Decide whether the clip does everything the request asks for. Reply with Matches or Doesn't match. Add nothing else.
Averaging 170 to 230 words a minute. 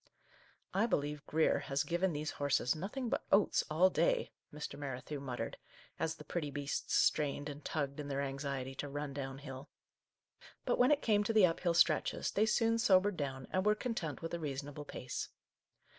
Matches